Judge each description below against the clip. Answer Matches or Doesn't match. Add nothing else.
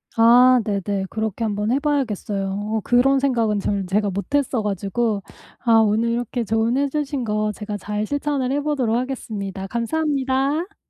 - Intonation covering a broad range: Doesn't match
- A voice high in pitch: Matches